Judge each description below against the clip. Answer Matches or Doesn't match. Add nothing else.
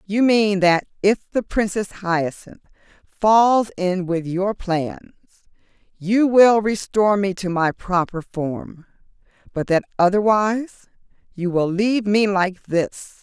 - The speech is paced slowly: Matches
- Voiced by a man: Doesn't match